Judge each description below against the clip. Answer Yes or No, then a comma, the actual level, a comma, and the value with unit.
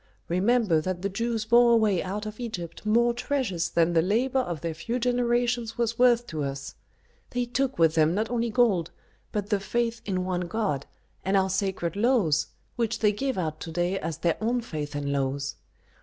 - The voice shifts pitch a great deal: Yes, wide, 5.9 semitones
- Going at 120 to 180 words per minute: No, average, 190 wpm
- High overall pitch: Yes, high, 205 Hz